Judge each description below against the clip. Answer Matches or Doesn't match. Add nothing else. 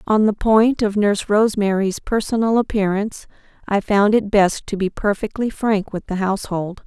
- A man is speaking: Doesn't match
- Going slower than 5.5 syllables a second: Matches